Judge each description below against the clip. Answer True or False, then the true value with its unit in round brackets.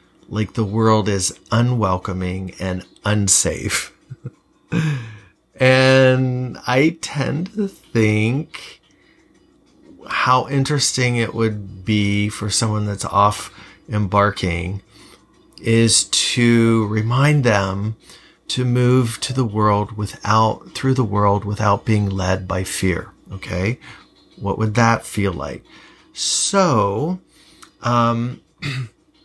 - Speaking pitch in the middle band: False (110 Hz)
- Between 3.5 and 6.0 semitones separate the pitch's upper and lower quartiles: True (4.0 semitones)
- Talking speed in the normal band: False (100 wpm)